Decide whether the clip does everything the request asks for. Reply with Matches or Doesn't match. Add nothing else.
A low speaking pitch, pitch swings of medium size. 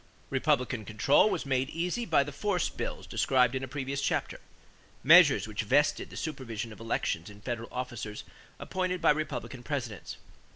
Matches